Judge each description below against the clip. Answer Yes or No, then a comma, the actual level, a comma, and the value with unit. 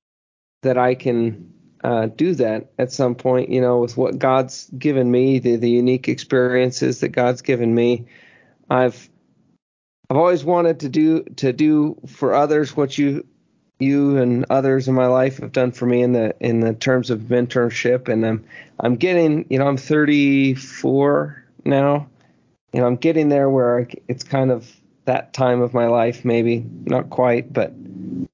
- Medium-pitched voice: No, low, 125 Hz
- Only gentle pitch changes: Yes, narrow, 2.3 semitones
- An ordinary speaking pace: Yes, average, 170 wpm